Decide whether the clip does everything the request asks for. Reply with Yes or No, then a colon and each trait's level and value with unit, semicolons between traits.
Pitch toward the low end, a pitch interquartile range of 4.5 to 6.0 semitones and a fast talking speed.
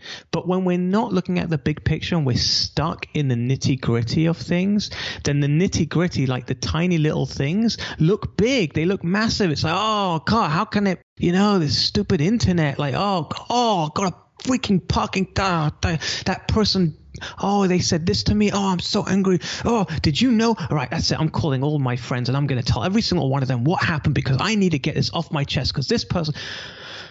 No: medium, 170 Hz; average, 5.3 semitones; fast, 220 wpm